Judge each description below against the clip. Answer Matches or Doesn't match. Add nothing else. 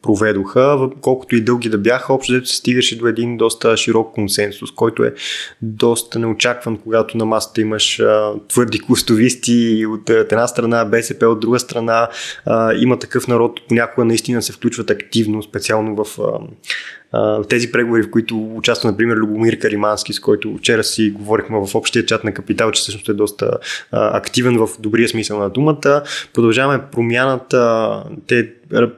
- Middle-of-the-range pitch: Doesn't match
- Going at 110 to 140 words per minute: Doesn't match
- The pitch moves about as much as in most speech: Doesn't match